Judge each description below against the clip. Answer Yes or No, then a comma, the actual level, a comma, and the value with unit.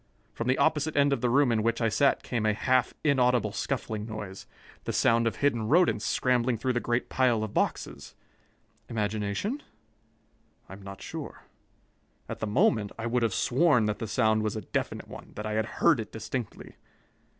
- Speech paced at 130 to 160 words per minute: No, average, 185 wpm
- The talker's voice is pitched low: Yes, low, 115 Hz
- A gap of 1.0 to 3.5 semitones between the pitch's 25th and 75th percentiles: Yes, average, 3.1 semitones